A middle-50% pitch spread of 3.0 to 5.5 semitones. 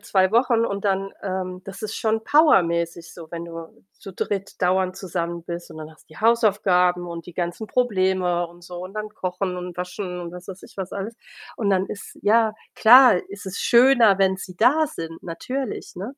Yes: average, 3.3 semitones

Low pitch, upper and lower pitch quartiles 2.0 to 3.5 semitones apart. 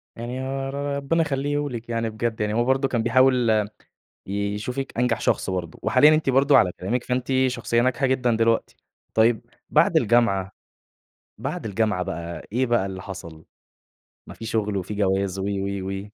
No: low, 115 Hz; average, 4.5 semitones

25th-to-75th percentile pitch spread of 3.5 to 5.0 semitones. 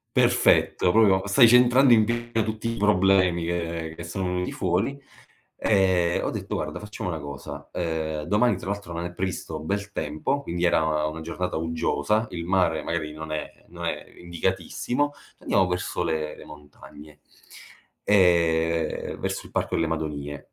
Yes: average, 4.0 semitones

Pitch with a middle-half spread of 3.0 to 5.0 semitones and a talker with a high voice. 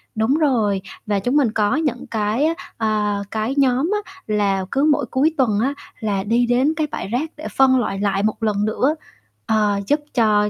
Yes: average, 4.5 semitones; high, 225 Hz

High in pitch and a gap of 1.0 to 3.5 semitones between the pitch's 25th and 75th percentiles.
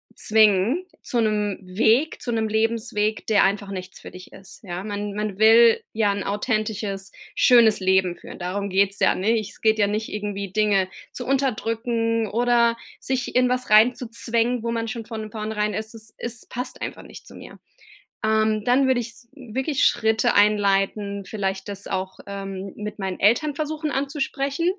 Yes: high, 215 Hz; average, 2.8 semitones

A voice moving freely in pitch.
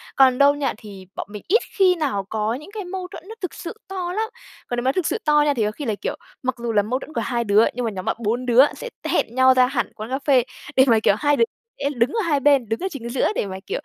No: average, 5.0 semitones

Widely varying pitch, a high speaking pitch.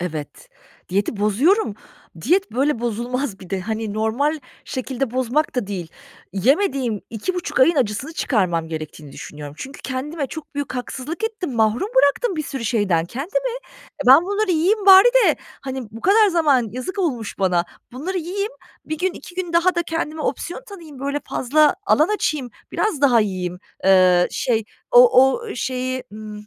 Yes: wide, 7.8 semitones; very high, 265 Hz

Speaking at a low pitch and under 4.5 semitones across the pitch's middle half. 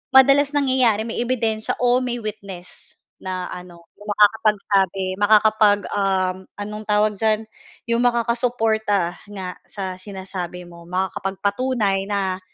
No: high, 205 Hz; average, 3.0 semitones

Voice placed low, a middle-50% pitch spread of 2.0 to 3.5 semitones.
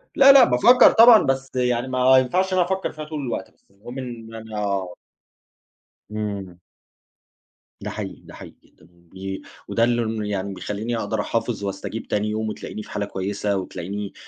No: low, 110 Hz; average, 4.3 semitones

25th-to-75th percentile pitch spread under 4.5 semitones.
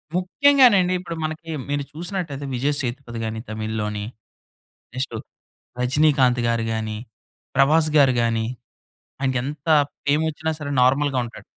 No: average, 5.0 semitones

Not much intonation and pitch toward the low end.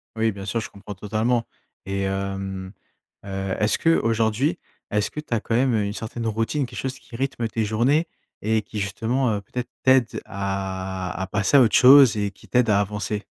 No: average, 3.6 semitones; low, 110 Hz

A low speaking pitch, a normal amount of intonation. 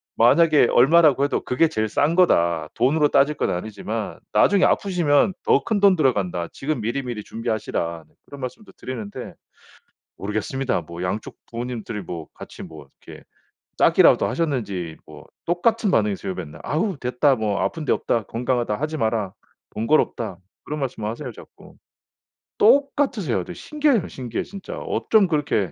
No: low, 125 Hz; wide, 7.1 semitones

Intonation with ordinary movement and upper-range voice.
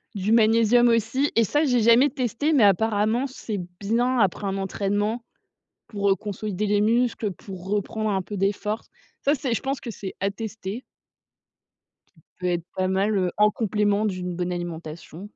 Yes: average, 3.0 semitones; high, 210 Hz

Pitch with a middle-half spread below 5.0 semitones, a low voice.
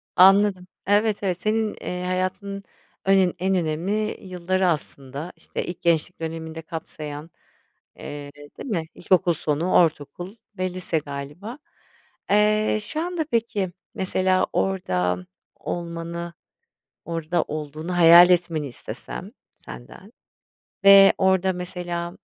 No: average, 3.0 semitones; medium, 180 Hz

